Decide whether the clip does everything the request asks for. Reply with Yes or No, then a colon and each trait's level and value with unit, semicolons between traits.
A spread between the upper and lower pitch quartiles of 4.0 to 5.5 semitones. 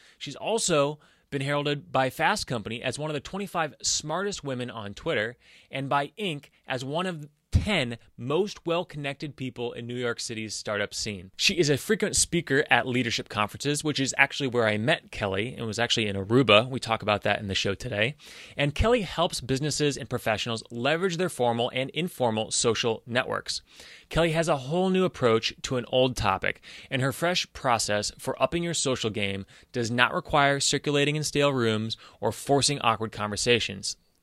Yes: average, 4.9 semitones